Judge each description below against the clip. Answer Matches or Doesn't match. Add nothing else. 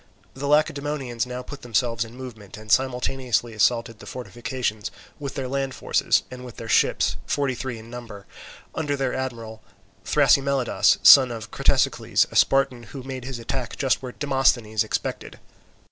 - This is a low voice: Matches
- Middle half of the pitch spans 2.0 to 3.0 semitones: Matches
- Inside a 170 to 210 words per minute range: Doesn't match